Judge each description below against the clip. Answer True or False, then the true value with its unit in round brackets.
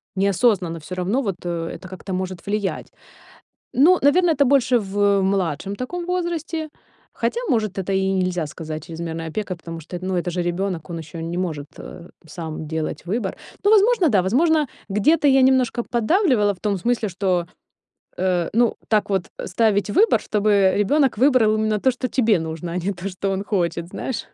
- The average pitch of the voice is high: True (200 Hz)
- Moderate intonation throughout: False (5.9 semitones)